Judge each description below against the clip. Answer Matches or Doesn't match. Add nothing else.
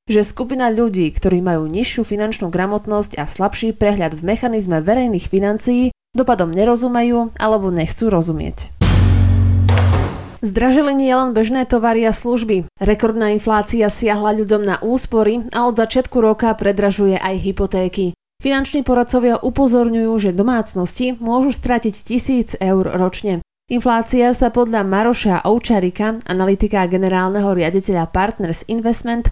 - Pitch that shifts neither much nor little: Matches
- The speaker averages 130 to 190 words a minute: Doesn't match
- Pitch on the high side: Matches